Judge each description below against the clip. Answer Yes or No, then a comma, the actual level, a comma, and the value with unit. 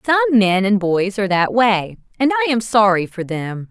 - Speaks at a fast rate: Yes, fast, 210 wpm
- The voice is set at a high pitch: Yes, high, 215 Hz